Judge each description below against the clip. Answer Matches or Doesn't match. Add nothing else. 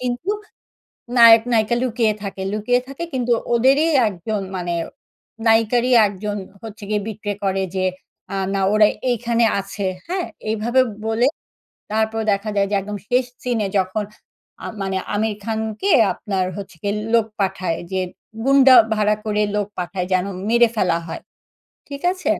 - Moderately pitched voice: Doesn't match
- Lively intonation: Doesn't match